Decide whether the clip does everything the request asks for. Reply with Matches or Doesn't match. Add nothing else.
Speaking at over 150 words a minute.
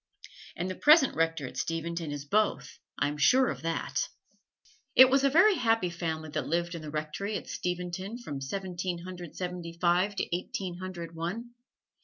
Matches